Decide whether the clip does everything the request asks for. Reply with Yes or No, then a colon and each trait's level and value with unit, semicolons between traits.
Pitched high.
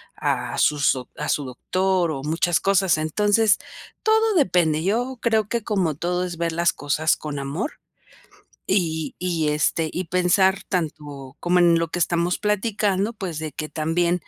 No: medium, 175 Hz